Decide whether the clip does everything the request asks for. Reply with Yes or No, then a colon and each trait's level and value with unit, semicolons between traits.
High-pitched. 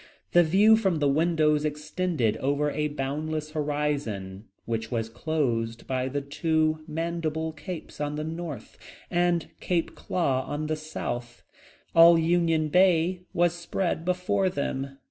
No: medium, 155 Hz